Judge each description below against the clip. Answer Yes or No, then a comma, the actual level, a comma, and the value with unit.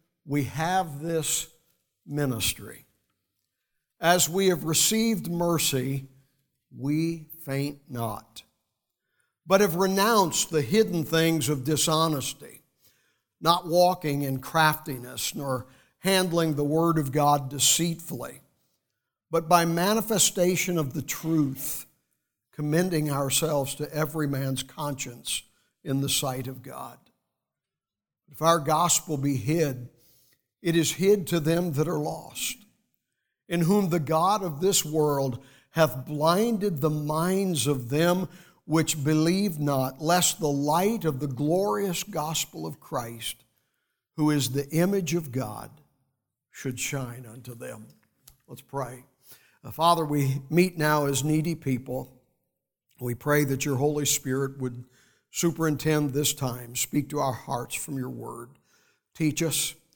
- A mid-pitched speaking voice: Yes, medium, 155 Hz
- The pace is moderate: No, slow, 125 wpm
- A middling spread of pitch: Yes, average, 3.6 semitones